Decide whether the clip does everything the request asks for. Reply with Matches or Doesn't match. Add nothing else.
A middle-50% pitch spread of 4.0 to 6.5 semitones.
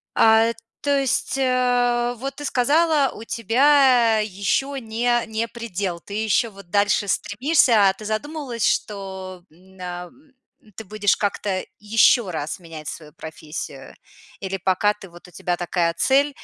Matches